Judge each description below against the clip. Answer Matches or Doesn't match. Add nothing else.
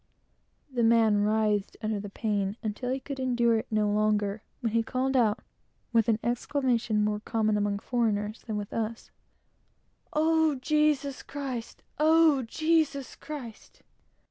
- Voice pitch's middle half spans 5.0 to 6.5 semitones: Doesn't match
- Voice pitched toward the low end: Doesn't match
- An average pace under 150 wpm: Matches